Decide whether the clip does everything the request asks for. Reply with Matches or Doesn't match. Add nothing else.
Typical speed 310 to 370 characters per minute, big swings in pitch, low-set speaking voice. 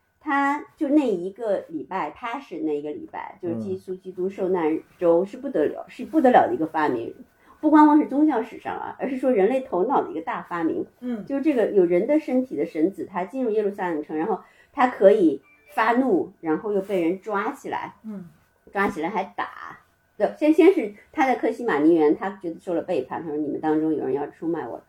Doesn't match